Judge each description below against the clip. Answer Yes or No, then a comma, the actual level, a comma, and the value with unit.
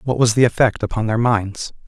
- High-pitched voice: No, low, 115 Hz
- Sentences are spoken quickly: Yes, fast, 225 wpm